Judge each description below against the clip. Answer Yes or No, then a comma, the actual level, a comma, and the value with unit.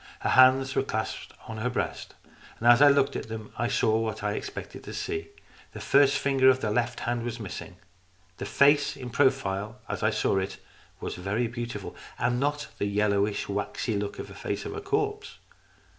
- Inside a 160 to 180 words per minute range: No, average, 200 wpm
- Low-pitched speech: Yes, low, 120 Hz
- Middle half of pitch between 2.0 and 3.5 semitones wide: No, average, 4.2 semitones